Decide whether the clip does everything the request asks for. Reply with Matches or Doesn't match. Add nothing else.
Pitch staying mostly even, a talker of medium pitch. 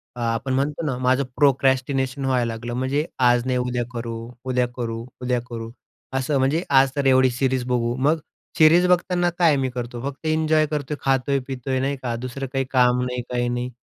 Doesn't match